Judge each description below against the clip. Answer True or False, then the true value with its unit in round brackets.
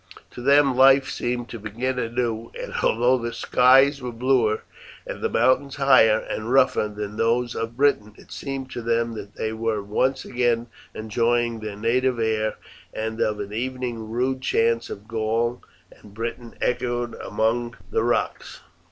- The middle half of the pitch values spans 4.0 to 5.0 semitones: False (2.4 semitones)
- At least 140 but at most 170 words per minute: True (160 wpm)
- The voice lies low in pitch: True (115 Hz)